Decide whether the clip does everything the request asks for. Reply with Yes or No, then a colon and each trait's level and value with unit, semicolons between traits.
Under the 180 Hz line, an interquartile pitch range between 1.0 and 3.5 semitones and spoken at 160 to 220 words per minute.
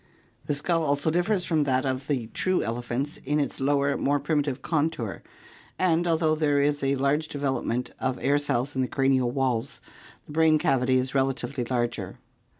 Yes: medium, 140 Hz; average, 2.7 semitones; average, 170 wpm